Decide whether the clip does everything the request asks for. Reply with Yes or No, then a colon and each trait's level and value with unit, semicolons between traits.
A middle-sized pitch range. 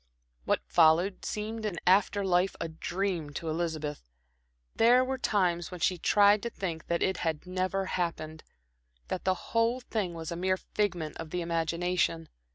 Yes: average, 3.4 semitones